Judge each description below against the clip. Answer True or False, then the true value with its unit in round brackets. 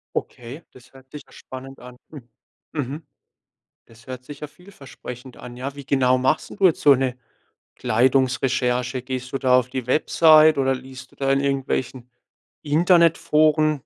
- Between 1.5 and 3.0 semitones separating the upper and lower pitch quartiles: True (2.6 semitones)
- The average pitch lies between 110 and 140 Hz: True (135 Hz)